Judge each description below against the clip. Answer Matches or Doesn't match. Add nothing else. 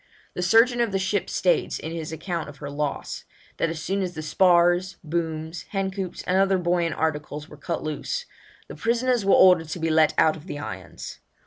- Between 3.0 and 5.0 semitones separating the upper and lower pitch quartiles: Matches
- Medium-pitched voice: Matches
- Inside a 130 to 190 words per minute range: Doesn't match